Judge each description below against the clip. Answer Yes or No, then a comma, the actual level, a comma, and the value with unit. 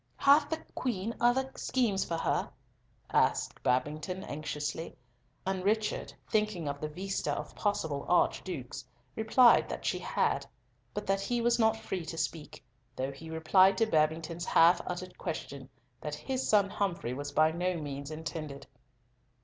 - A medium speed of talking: Yes, average, 150 wpm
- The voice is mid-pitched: Yes, medium, 180 Hz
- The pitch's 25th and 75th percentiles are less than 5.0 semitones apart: No, wide, 5.5 semitones